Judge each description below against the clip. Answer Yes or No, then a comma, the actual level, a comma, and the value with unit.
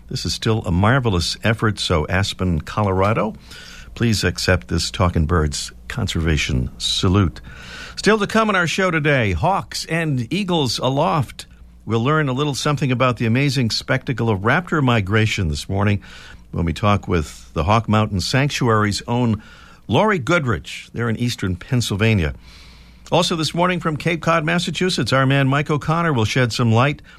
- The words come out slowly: No, average, 155 wpm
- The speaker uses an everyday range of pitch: No, wide, 7.9 semitones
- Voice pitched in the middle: No, low, 115 Hz